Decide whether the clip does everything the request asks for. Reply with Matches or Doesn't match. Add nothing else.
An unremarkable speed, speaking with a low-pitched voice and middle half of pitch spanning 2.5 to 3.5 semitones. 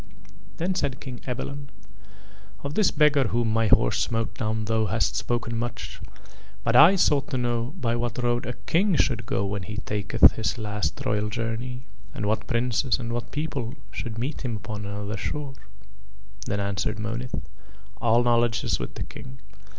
Matches